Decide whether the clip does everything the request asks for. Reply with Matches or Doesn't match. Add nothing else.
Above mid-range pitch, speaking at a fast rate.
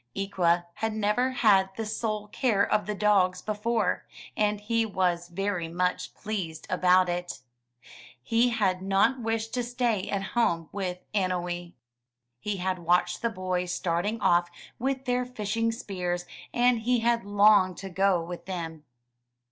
Doesn't match